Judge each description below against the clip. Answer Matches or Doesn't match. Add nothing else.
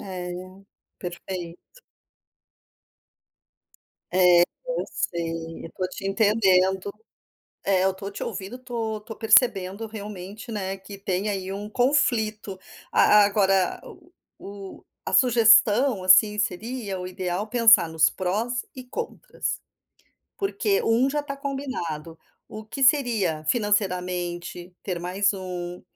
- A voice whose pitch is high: Matches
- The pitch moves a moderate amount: Matches